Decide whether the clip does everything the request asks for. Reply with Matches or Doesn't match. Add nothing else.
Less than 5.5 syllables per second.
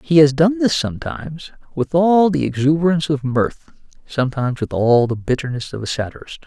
Doesn't match